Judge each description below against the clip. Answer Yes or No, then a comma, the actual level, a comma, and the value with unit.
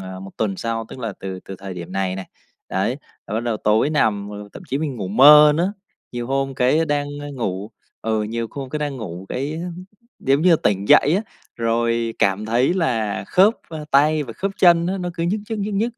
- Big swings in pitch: Yes, wide, 6.4 semitones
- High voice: No, low, 125 Hz